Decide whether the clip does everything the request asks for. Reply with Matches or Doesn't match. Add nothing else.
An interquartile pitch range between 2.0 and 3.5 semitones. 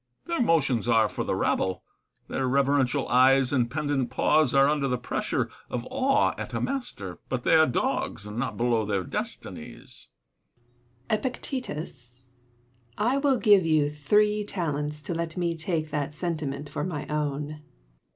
Doesn't match